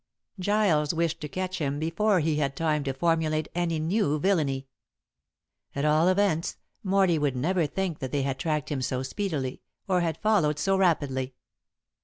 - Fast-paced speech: No, average, 165 wpm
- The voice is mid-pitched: Yes, medium, 160 Hz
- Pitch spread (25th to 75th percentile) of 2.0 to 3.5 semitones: No, average, 4.2 semitones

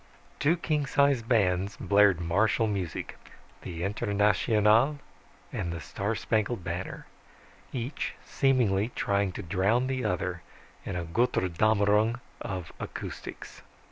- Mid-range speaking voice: No, low, 105 Hz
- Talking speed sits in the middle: No, slow, 115 wpm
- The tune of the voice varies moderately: Yes, average, 4.2 semitones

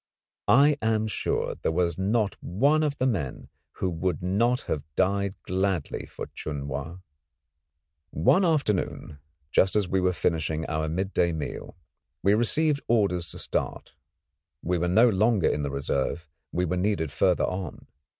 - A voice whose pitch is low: Yes, very low, 95 Hz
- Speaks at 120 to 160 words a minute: Yes, average, 150 wpm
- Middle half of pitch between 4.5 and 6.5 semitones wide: Yes, average, 4.8 semitones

